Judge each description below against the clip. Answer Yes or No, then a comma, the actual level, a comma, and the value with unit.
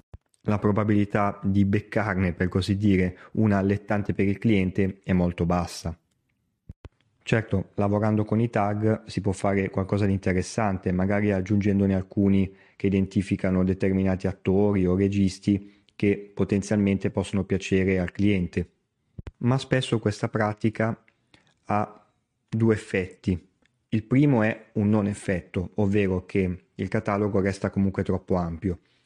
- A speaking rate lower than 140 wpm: Yes, average, 130 wpm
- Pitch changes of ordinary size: No, narrow, 1.7 semitones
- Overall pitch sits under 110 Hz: Yes, low, 100 Hz